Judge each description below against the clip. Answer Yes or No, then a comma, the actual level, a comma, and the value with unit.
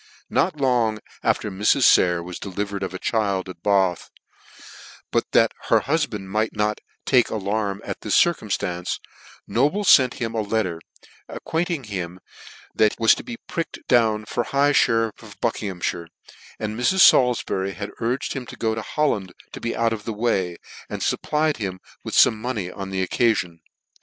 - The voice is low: Yes, low, 110 Hz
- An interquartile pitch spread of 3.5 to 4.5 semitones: Yes, average, 4.2 semitones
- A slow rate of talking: No, average, 170 wpm